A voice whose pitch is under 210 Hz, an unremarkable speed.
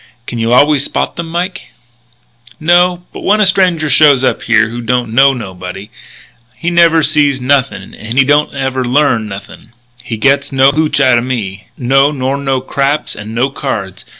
Yes: low, 135 Hz; average, 175 wpm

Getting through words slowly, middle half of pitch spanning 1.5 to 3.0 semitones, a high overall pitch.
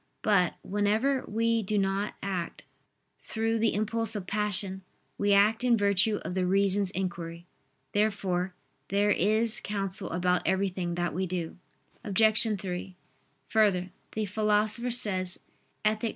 Yes: slow, 130 wpm; average, 2.7 semitones; high, 200 Hz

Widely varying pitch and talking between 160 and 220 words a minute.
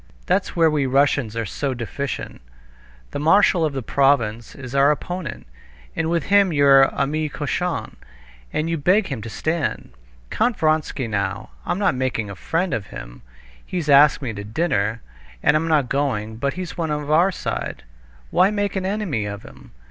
Yes: wide, 6.3 semitones; average, 170 wpm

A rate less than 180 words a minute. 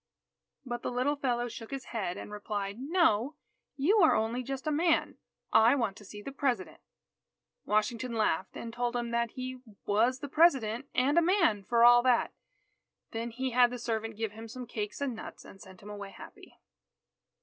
No: average, 185 wpm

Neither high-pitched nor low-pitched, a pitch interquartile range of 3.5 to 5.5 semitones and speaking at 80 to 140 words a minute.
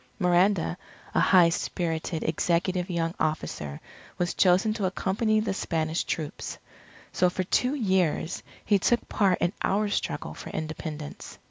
No: medium, 180 Hz; average, 3.1 semitones; slow, 135 wpm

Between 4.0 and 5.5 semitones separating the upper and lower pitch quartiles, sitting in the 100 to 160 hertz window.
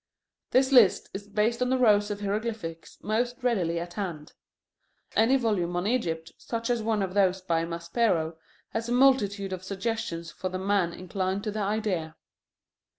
No: average, 4.4 semitones; high, 200 Hz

